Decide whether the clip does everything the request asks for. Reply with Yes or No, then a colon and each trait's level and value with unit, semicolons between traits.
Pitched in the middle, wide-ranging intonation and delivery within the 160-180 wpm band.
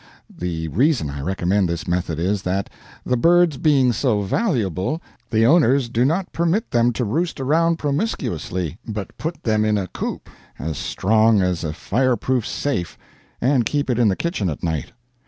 No: low, 115 Hz; wide, 7.7 semitones; average, 170 wpm